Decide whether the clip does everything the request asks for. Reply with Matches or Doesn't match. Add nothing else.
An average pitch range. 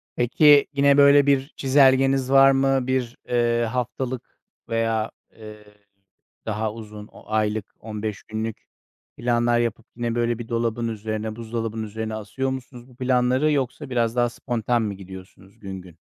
Matches